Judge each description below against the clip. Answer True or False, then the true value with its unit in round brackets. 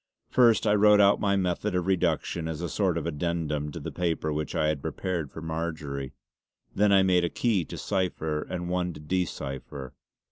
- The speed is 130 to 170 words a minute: False (200 wpm)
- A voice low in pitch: True (85 Hz)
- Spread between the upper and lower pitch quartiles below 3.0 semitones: False (3.5 semitones)